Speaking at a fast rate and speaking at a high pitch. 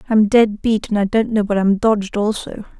Yes: fast, 235 wpm; high, 210 Hz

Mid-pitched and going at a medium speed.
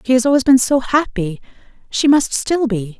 No: very high, 250 Hz; average, 180 wpm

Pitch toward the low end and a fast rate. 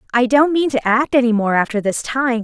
No: high, 245 Hz; fast, 245 wpm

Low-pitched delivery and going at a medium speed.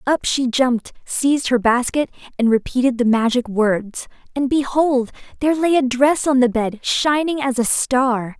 No: very high, 255 Hz; average, 170 wpm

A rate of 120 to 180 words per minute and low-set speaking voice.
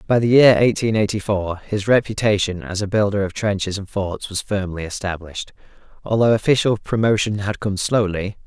Yes: average, 170 wpm; low, 100 Hz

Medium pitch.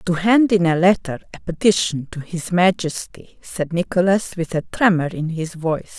Yes: medium, 175 Hz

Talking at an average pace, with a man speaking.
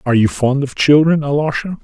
Yes: average, 195 wpm; male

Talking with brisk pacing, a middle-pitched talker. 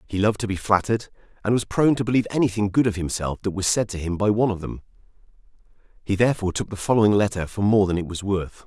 No: fast, 240 wpm; low, 100 Hz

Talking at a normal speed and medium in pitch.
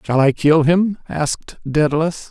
Yes: average, 155 wpm; medium, 155 Hz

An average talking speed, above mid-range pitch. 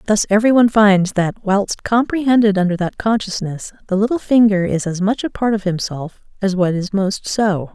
Yes: average, 195 wpm; high, 200 Hz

